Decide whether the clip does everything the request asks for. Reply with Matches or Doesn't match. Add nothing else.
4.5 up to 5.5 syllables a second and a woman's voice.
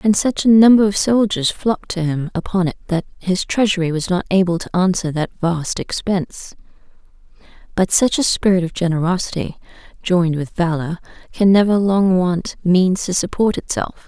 Matches